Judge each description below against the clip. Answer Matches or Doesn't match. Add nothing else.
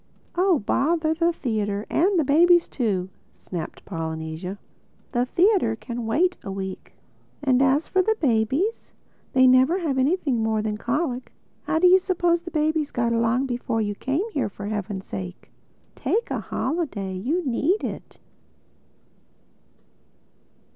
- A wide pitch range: Matches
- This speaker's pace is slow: Matches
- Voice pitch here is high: Matches